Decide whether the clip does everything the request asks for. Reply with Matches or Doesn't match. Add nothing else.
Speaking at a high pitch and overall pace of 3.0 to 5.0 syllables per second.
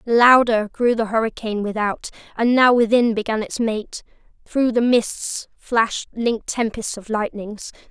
Matches